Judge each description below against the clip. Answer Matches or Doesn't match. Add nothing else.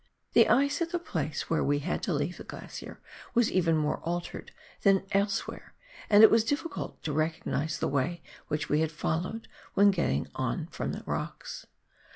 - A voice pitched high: Doesn't match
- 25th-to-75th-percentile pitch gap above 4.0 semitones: Matches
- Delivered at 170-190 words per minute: Matches